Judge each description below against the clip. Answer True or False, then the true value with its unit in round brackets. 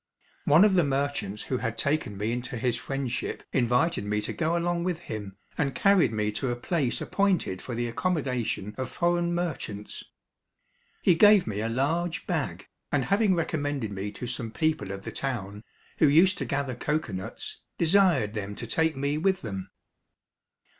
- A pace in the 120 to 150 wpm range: False (175 wpm)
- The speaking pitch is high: False (135 Hz)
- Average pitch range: False (7.1 semitones)